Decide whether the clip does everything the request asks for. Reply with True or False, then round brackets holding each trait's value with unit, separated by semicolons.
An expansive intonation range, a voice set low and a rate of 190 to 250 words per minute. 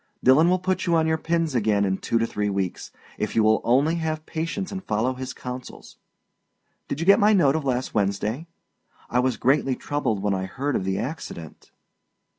True (6.7 semitones; 130 Hz; 200 wpm)